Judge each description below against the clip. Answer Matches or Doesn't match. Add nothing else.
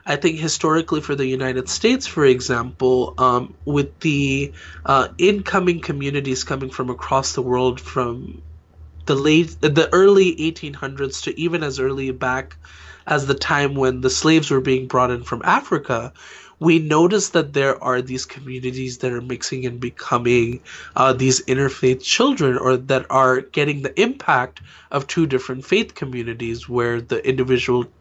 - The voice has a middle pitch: Doesn't match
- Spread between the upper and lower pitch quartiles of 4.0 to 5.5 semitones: Doesn't match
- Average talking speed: Matches